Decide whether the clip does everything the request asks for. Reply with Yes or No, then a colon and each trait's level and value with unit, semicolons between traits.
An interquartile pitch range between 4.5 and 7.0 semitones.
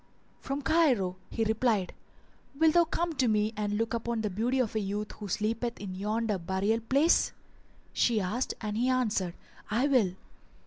No: average, 3.5 semitones